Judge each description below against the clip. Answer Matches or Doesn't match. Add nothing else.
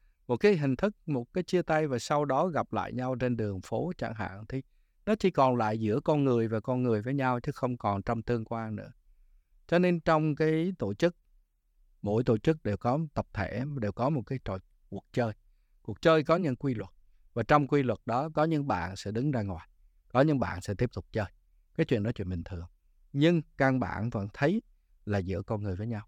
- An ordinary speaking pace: Matches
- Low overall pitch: Matches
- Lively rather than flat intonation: Matches